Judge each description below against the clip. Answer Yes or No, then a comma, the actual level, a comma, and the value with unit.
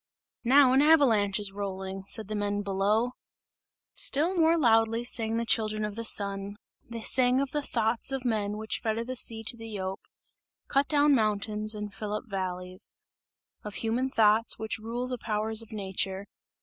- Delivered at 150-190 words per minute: Yes, average, 175 wpm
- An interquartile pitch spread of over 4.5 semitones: No, average, 3.1 semitones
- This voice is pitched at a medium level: No, high, 220 Hz